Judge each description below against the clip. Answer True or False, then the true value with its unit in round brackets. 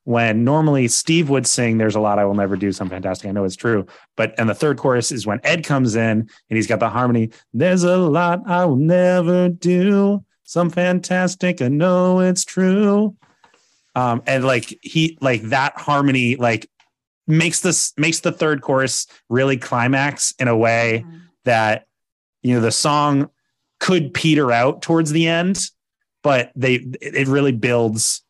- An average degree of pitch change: False (6.7 semitones)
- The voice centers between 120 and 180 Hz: True (135 Hz)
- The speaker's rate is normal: True (170 wpm)